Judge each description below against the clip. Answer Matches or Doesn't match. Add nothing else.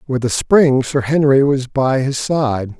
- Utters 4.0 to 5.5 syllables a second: Doesn't match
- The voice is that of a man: Matches